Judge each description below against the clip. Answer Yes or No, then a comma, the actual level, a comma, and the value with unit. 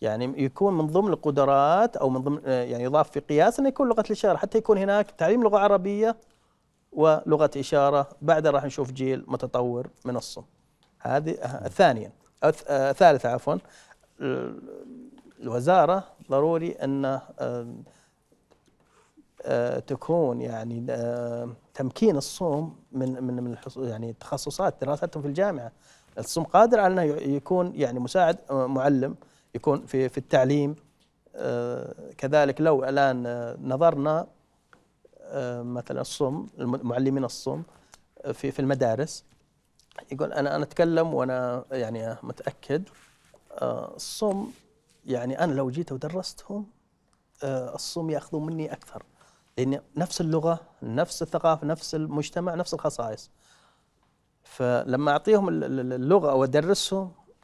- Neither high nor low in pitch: Yes, medium, 145 Hz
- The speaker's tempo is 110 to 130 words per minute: Yes, average, 115 wpm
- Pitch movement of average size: Yes, average, 4.9 semitones